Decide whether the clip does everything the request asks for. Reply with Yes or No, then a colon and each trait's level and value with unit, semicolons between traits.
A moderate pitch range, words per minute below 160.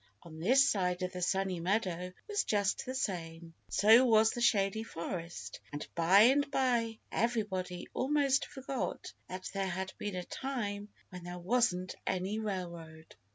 Yes: average, 4.6 semitones; average, 150 wpm